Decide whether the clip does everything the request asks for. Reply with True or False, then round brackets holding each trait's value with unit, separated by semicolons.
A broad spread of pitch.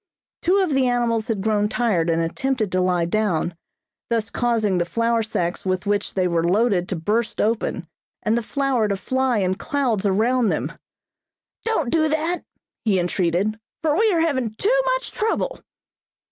True (5.7 semitones)